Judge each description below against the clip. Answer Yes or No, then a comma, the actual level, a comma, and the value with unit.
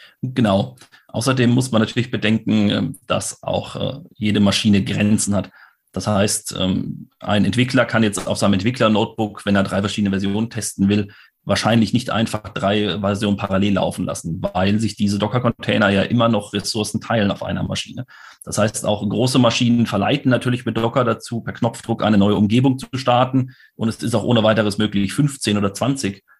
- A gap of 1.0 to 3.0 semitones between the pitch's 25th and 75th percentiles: Yes, narrow, 2.5 semitones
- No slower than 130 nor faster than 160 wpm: No, average, 170 wpm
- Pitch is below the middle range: Yes, low, 105 Hz